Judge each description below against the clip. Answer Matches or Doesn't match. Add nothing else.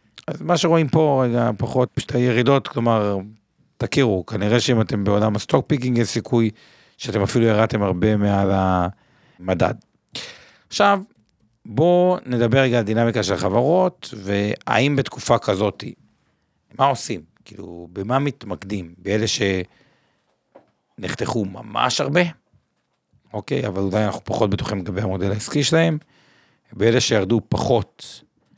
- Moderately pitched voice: Doesn't match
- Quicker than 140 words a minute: Doesn't match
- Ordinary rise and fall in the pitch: Matches